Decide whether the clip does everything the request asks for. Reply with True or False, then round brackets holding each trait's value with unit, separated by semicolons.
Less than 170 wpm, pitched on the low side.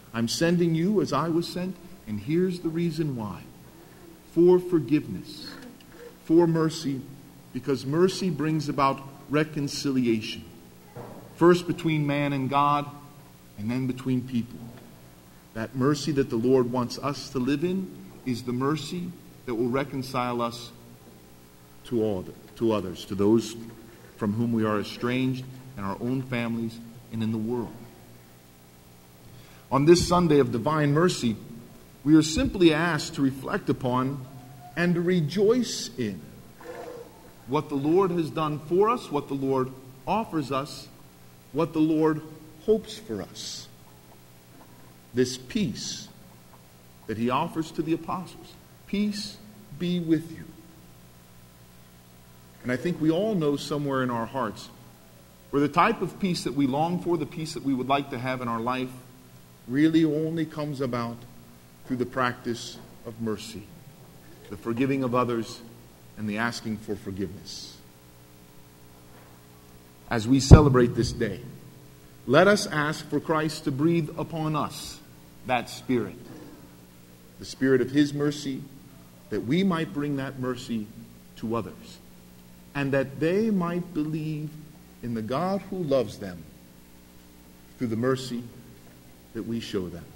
True (140 wpm; 130 Hz)